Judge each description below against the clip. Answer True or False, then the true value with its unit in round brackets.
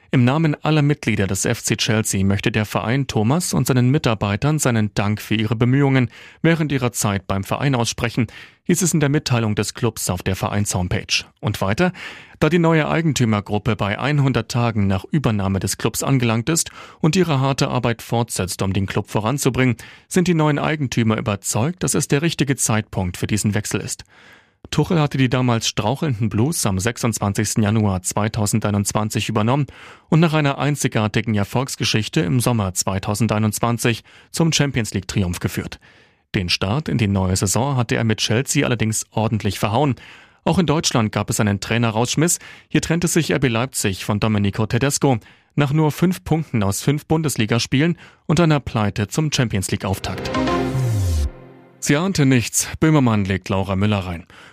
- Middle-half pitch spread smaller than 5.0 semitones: False (5.4 semitones)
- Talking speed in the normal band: True (160 wpm)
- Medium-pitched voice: False (115 Hz)